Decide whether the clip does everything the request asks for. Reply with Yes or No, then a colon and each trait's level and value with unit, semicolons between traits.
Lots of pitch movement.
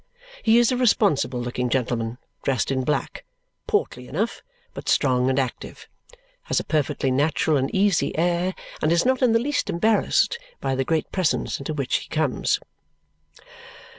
Yes: wide, 7.6 semitones